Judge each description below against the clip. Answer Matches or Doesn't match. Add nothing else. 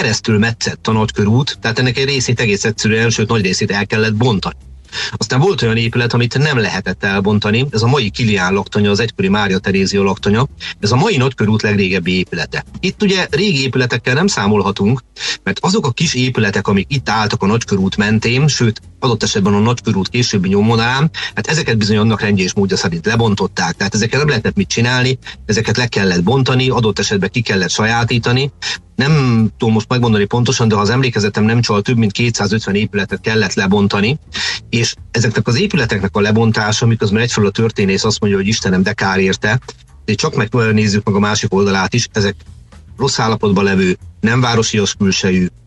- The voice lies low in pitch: Matches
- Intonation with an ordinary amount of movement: Matches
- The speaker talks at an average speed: Doesn't match